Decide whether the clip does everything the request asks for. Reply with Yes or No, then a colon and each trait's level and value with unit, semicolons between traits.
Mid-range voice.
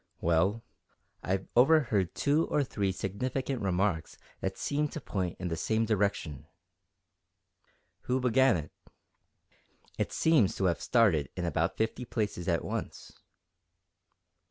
No: low, 100 Hz